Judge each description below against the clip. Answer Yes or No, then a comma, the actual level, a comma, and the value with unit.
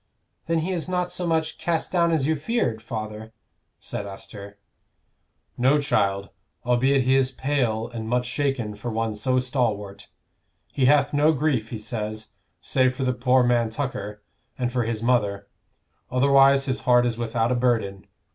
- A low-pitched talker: Yes, low, 125 Hz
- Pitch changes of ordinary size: Yes, average, 3.9 semitones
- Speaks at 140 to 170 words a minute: Yes, average, 165 wpm